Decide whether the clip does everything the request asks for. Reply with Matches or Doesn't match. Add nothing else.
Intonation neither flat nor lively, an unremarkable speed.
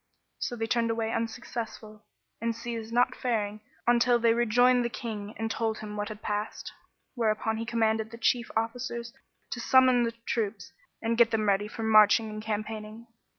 Doesn't match